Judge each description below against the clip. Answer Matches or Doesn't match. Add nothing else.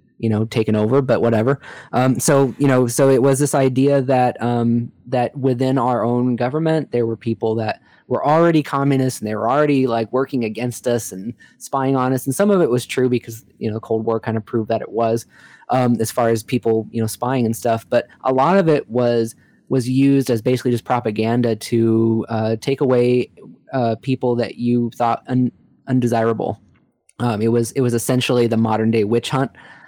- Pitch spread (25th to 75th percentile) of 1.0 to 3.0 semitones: Matches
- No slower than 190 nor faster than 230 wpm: Matches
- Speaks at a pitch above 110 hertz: Matches